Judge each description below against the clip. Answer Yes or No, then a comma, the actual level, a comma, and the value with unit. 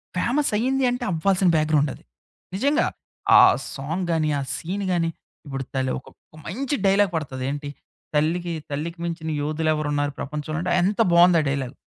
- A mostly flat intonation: No, average, 4.3 semitones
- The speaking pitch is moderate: Yes, medium, 165 Hz